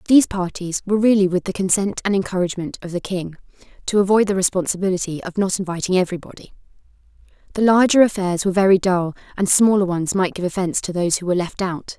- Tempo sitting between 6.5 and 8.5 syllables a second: Yes, 6.8 syllables/s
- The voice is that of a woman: Yes, female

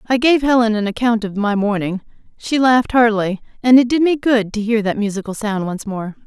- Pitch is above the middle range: Yes, high, 225 Hz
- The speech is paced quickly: Yes, fast, 220 wpm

